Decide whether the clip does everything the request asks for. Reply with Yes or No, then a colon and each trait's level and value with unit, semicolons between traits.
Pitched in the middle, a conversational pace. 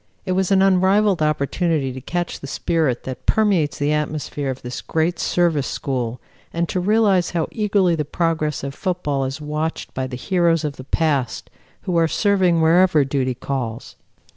Yes: medium, 160 Hz; average, 170 wpm